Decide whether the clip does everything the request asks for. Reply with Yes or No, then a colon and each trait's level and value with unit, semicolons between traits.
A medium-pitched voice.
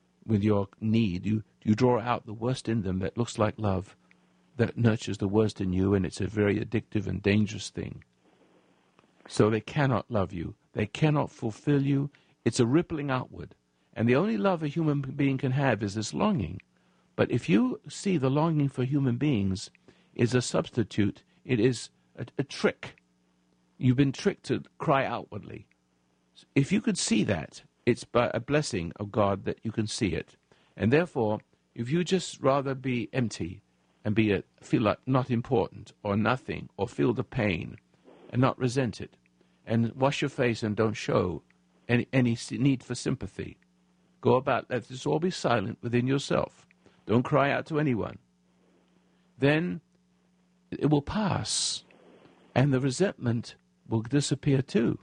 No: low, 120 Hz